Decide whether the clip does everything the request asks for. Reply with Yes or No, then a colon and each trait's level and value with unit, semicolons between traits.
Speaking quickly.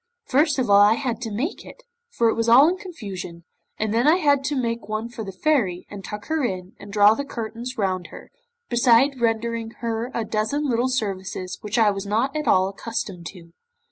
Yes: fast, 210 wpm